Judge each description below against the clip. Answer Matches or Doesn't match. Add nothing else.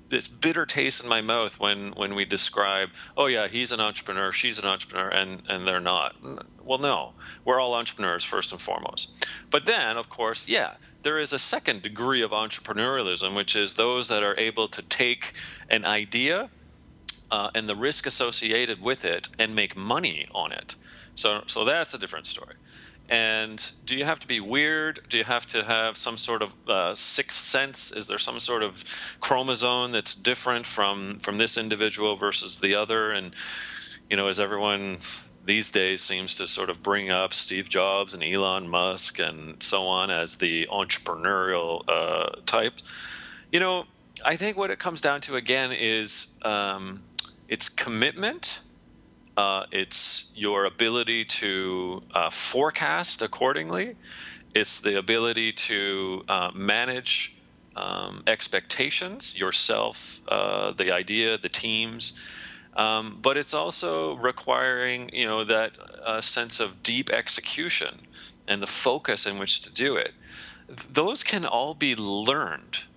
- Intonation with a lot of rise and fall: Doesn't match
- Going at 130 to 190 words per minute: Matches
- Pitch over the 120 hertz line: Doesn't match